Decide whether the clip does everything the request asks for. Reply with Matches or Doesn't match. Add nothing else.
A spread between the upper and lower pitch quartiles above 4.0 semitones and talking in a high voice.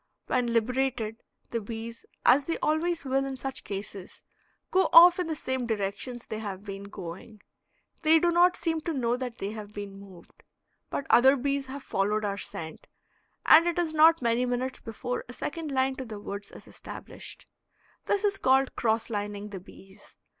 Matches